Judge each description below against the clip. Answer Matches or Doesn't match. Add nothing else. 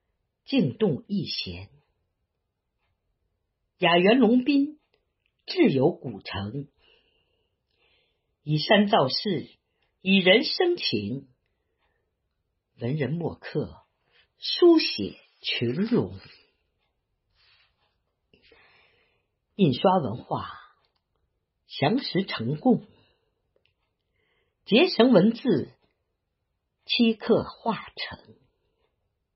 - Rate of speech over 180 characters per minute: Doesn't match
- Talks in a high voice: Matches